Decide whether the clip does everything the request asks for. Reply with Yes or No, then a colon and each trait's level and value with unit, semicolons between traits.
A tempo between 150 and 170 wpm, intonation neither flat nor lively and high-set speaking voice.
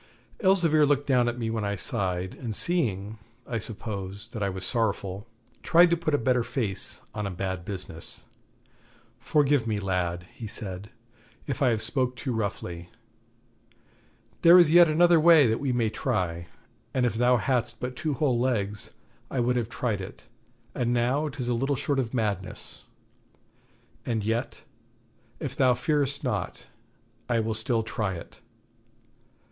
No: average, 155 wpm; average, 5.0 semitones; low, 120 Hz